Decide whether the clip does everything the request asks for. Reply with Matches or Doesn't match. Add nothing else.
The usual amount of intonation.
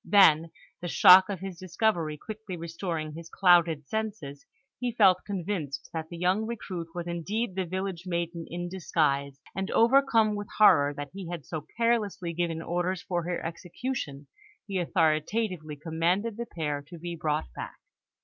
Matches